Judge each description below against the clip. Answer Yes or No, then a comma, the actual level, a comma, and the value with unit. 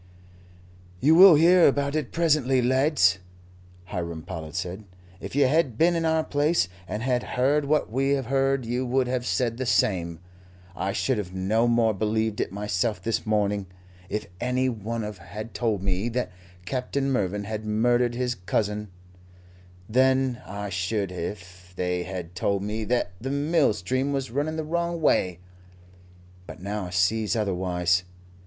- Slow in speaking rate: No, average, 160 wpm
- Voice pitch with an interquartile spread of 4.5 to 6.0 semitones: Yes, wide, 5.6 semitones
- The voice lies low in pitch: Yes, low, 115 Hz